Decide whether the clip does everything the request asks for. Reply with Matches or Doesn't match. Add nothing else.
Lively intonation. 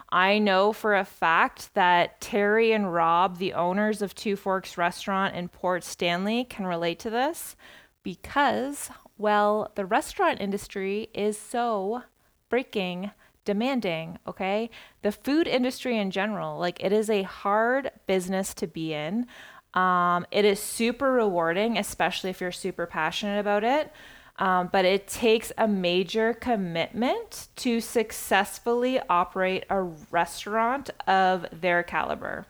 Doesn't match